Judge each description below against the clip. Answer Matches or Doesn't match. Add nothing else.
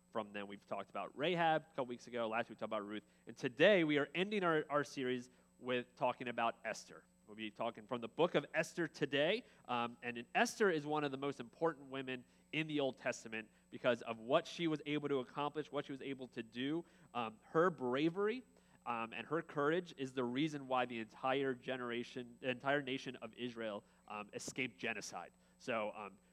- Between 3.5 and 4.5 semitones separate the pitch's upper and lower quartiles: Matches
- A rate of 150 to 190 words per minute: Doesn't match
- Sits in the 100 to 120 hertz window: Doesn't match